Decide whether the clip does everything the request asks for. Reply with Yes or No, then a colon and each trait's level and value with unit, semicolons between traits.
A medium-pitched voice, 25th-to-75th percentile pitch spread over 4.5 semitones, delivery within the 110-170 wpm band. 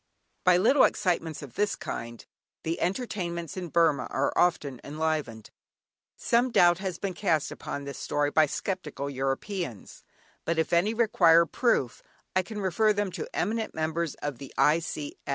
Yes: medium, 170 Hz; average, 4.9 semitones; average, 150 wpm